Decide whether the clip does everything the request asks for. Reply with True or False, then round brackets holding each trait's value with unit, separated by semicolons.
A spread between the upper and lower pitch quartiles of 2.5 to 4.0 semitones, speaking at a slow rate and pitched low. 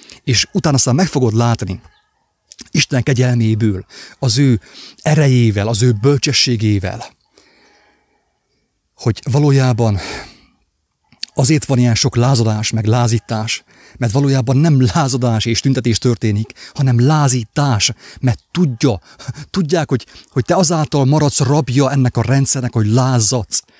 True (3.4 semitones; 115 wpm; 125 Hz)